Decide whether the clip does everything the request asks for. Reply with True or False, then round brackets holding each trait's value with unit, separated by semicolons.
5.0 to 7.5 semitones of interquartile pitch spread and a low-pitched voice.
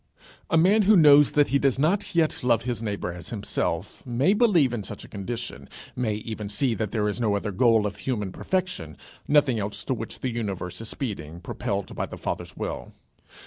True (5.6 semitones; 115 Hz)